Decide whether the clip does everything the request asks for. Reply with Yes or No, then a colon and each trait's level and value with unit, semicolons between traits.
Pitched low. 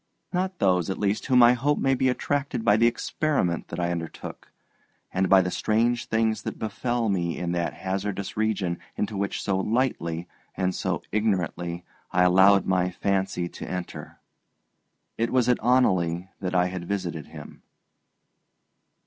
Yes: low, 100 Hz